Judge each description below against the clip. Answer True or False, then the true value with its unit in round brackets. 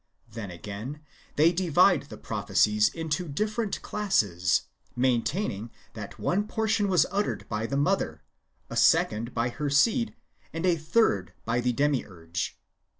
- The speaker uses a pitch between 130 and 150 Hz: True (140 Hz)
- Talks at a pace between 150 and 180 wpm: False (135 wpm)